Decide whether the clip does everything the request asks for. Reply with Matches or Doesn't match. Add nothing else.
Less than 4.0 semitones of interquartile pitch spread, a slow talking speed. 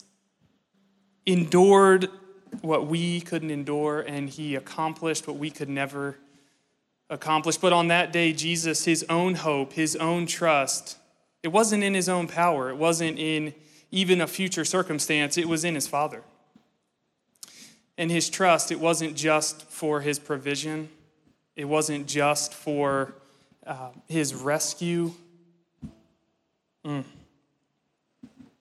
Matches